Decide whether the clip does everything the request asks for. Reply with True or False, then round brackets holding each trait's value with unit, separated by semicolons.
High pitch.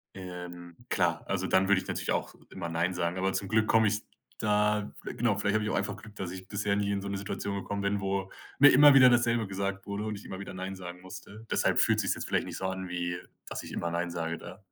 False (100 Hz)